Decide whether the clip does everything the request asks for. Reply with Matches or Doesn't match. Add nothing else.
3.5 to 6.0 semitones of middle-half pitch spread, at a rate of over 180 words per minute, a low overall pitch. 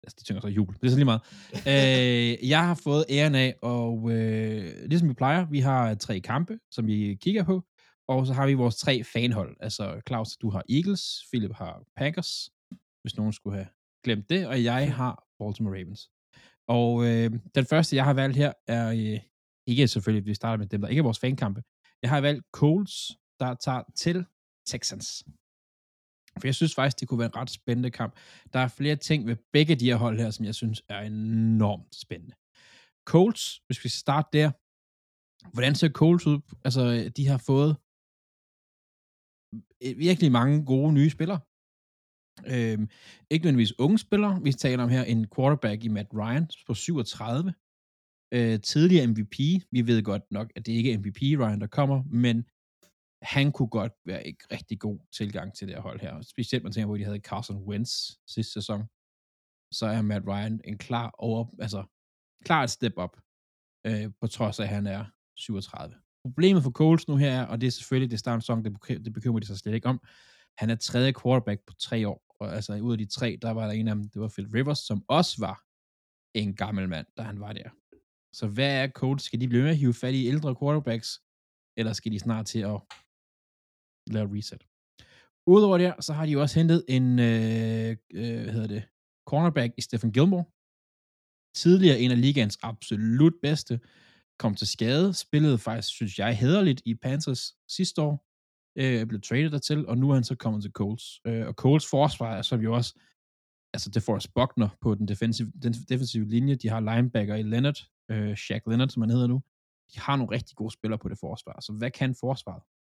Matches